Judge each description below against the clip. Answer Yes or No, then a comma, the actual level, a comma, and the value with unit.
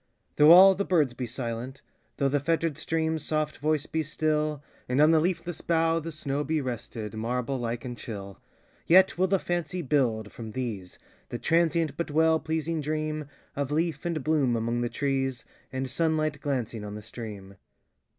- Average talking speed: Yes, average, 150 wpm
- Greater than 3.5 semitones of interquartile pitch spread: Yes, average, 4.6 semitones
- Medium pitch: Yes, medium, 145 Hz